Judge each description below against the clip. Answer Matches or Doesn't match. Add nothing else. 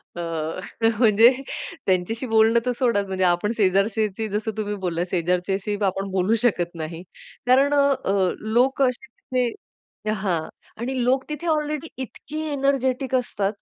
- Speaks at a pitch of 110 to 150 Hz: Doesn't match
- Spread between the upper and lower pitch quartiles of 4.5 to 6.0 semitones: Matches